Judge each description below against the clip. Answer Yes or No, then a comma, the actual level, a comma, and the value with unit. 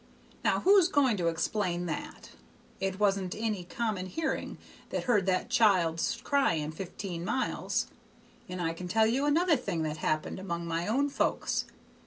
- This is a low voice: No, high, 195 Hz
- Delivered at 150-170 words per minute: Yes, average, 155 wpm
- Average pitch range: No, wide, 5.9 semitones